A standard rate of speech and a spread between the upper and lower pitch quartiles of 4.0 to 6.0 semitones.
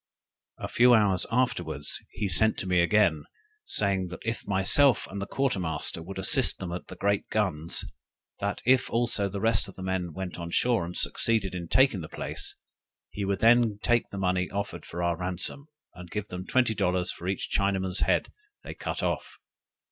No: average, 190 wpm; average, 3.4 semitones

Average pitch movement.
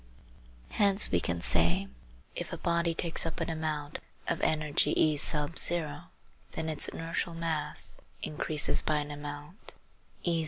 No: narrow, 2.1 semitones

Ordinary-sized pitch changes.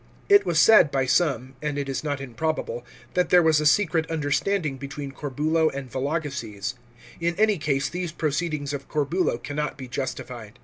Yes: average, 3.3 semitones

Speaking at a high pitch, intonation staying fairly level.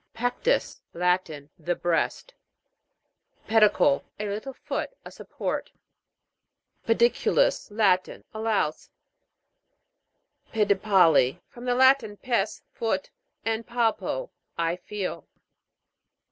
No: high, 215 Hz; average, 4.8 semitones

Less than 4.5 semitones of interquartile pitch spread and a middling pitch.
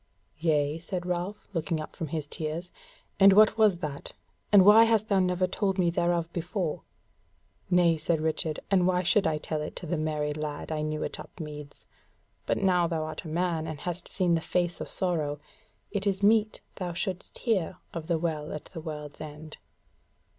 Yes: average, 3.1 semitones; medium, 170 Hz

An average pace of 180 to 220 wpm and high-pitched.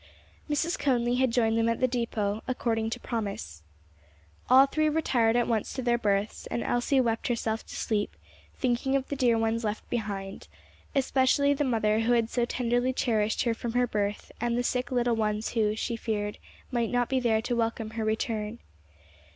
Yes: average, 185 wpm; high, 235 Hz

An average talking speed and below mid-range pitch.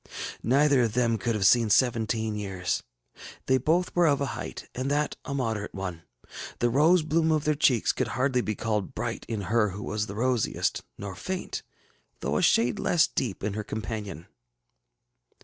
Yes: average, 180 wpm; low, 115 Hz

